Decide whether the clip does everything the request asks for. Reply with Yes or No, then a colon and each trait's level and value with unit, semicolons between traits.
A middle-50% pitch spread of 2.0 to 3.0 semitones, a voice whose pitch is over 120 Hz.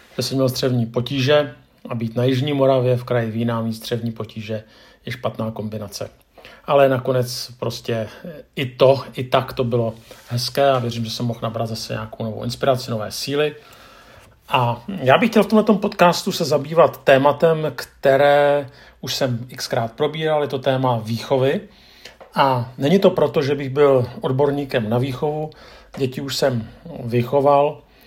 No: average, 3.4 semitones; low, 130 Hz